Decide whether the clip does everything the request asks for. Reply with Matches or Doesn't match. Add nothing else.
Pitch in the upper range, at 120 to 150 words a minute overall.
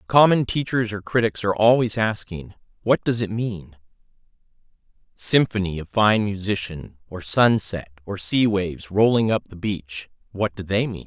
Doesn't match